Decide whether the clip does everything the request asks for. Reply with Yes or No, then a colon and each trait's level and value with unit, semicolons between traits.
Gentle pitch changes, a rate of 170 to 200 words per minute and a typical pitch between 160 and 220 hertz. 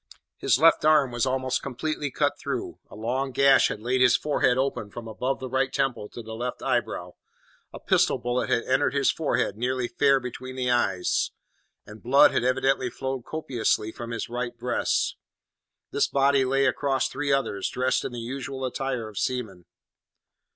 No: narrow, 2.2 semitones; average, 175 wpm; low, 130 Hz